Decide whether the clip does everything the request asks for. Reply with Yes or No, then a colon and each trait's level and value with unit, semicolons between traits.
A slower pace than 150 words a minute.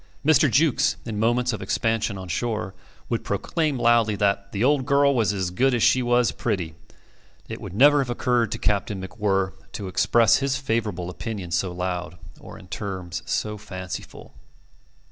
No: average, 165 wpm